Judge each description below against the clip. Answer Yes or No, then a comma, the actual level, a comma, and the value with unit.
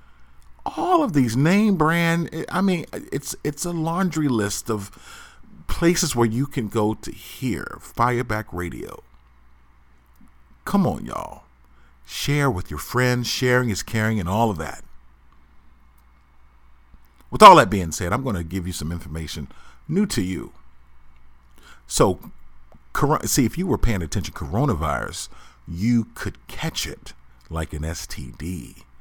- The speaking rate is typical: No, slow, 130 wpm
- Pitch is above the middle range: No, very low, 90 Hz